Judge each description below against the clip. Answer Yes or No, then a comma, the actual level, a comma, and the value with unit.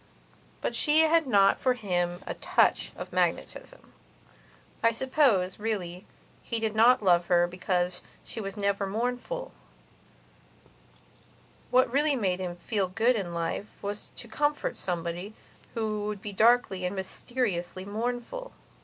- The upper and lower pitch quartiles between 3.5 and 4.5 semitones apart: No, average, 5.1 semitones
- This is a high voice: Yes, high, 210 Hz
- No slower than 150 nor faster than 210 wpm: No, slow, 135 wpm